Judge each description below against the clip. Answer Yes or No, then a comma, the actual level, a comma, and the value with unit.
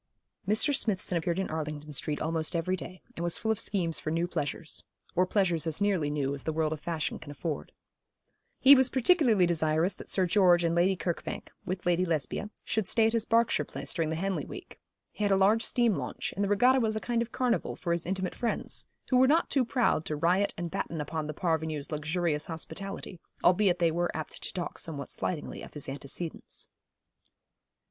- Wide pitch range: No, average, 4.3 semitones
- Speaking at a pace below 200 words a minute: No, fast, 205 wpm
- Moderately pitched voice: Yes, medium, 175 Hz